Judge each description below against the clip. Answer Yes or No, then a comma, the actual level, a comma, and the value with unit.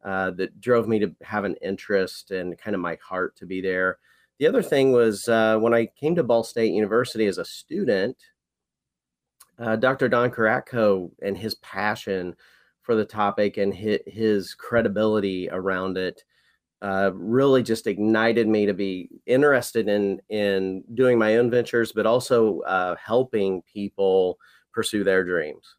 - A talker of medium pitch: No, low, 105 Hz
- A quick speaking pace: No, average, 160 wpm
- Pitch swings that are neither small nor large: Yes, average, 3.4 semitones